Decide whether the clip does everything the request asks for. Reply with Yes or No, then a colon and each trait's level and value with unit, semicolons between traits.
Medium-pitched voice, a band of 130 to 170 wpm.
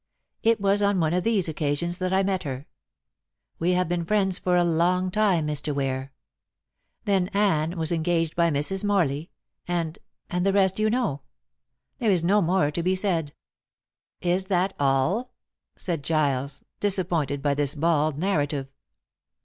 Yes: medium, 175 Hz; average, 155 wpm